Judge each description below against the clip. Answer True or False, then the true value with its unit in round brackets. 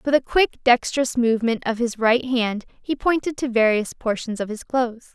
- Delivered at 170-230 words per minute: True (200 wpm)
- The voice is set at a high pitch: True (240 Hz)